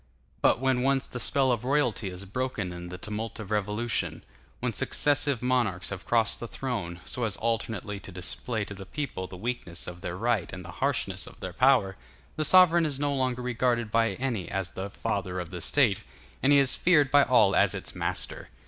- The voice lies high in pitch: No, low, 115 Hz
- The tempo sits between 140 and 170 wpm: No, average, 200 wpm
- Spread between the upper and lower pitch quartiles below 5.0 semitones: No, average, 5.3 semitones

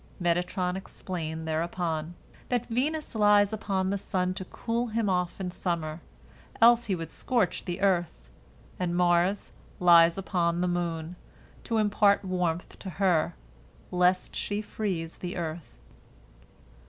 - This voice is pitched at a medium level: Yes, medium, 180 Hz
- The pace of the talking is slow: Yes, slow, 130 wpm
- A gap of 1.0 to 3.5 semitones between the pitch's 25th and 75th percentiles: Yes, average, 3.0 semitones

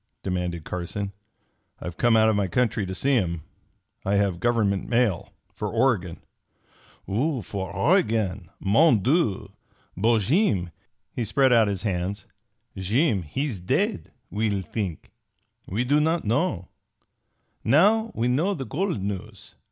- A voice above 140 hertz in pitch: No, low, 105 Hz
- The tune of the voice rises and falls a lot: Yes, wide, 5.7 semitones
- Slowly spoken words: Yes, slow, 130 wpm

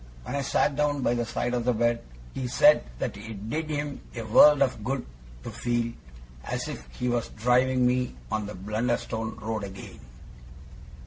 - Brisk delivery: No, average, 180 wpm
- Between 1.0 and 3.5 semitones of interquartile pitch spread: Yes, average, 2.8 semitones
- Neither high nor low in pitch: No, low, 120 Hz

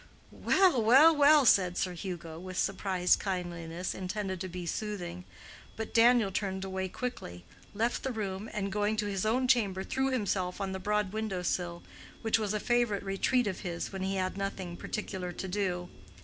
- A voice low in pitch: No, high, 195 Hz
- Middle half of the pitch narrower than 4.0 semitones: Yes, average, 3.1 semitones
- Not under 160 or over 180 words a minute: Yes, average, 175 wpm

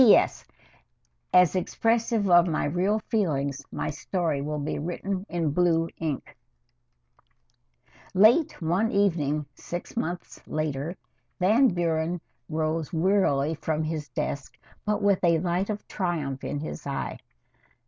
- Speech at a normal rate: No, slow, 130 wpm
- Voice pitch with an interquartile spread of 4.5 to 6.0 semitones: No, average, 4.0 semitones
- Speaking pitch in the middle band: Yes, medium, 170 Hz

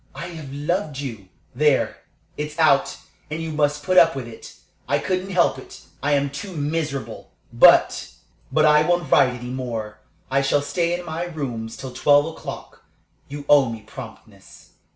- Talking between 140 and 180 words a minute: Yes, average, 170 wpm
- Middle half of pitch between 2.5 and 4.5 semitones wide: Yes, average, 3.6 semitones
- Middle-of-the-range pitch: Yes, medium, 145 Hz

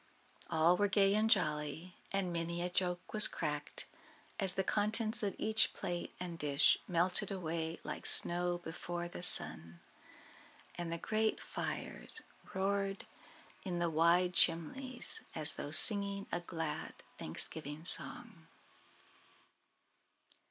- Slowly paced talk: Yes, slow, 125 wpm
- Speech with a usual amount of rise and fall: Yes, average, 3.2 semitones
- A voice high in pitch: No, medium, 175 Hz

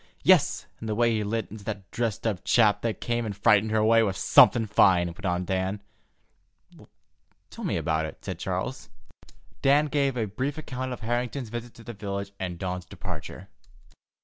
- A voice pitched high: No, low, 110 Hz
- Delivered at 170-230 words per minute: Yes, average, 180 wpm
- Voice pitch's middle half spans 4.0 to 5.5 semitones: No, average, 3.4 semitones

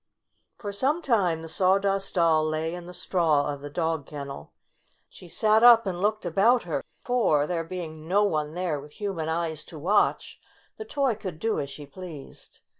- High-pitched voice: No, medium, 175 Hz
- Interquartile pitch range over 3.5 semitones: Yes, average, 4.5 semitones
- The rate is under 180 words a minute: No, average, 185 wpm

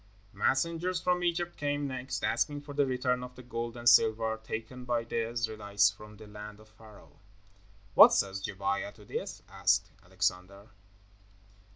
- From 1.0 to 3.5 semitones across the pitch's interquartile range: No, average, 4.0 semitones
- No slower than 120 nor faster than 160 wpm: Yes, average, 155 wpm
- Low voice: Yes, low, 115 Hz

